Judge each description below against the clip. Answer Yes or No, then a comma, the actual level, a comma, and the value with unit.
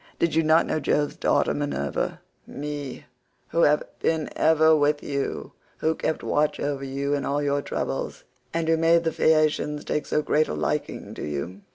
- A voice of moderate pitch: Yes, medium, 150 Hz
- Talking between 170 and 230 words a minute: Yes, average, 175 wpm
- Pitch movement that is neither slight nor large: No, narrow, 2.0 semitones